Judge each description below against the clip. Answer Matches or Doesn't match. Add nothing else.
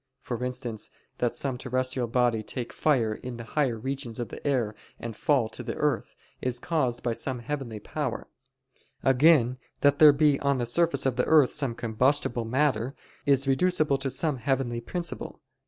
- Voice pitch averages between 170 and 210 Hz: Doesn't match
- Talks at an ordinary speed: Matches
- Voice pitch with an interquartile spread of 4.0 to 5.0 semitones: Doesn't match